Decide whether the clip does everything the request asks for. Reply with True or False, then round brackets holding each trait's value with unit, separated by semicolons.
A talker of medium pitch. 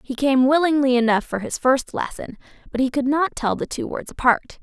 False (265 Hz)